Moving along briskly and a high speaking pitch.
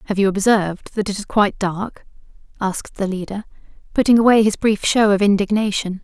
No: average, 180 wpm; high, 205 Hz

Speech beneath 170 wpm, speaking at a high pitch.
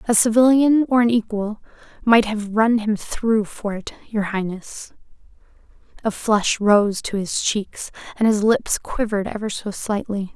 Yes: average, 155 wpm; high, 215 Hz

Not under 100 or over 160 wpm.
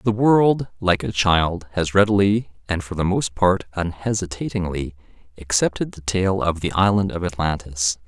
Yes: average, 155 wpm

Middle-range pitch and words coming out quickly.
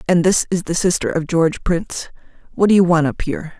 Yes: medium, 170 Hz; fast, 215 wpm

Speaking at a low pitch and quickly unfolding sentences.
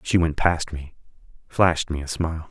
No: very low, 80 Hz; average, 190 wpm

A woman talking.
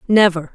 Yes: female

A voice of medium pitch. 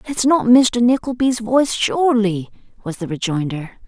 No: high, 225 Hz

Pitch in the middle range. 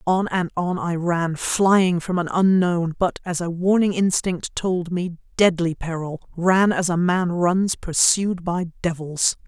Yes: medium, 175 Hz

